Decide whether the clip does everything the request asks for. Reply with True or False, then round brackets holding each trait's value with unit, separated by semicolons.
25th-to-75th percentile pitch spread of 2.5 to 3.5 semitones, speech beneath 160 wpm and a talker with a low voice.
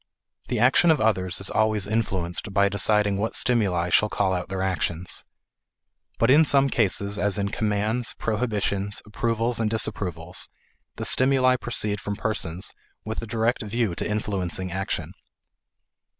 True (2.9 semitones; 145 wpm; 105 Hz)